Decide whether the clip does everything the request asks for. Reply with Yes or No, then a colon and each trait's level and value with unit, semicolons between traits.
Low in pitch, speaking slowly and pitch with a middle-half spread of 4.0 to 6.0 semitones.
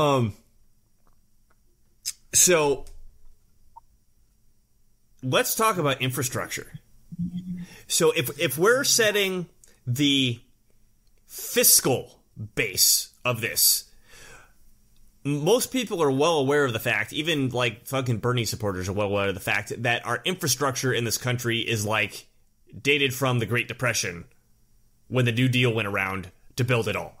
Yes: low, 120 Hz; slow, 130 wpm; average, 4.6 semitones